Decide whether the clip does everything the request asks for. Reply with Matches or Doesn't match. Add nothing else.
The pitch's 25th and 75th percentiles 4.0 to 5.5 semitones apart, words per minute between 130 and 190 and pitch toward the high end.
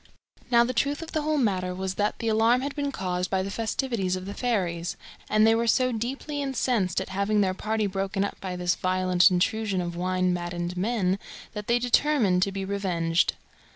Doesn't match